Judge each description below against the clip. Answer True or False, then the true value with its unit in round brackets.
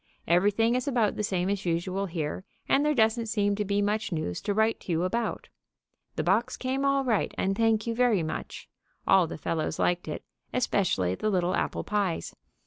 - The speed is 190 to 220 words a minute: True (195 wpm)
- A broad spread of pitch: False (4.3 semitones)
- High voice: True (205 Hz)